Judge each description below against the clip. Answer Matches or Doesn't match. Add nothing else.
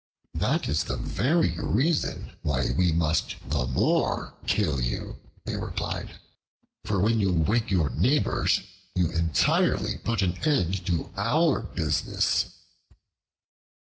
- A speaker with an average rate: Doesn't match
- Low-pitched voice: Matches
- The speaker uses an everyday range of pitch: Doesn't match